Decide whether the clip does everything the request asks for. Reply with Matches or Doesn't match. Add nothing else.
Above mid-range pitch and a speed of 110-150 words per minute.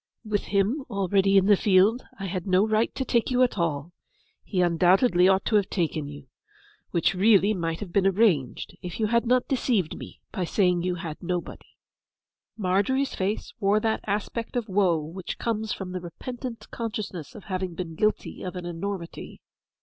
Doesn't match